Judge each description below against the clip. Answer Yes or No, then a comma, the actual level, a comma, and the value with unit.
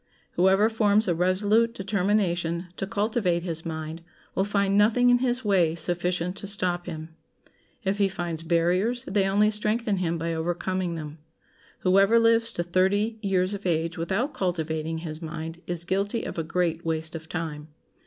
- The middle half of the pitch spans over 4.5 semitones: No, average, 3.5 semitones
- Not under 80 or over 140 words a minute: No, average, 165 wpm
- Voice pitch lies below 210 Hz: Yes, medium, 185 Hz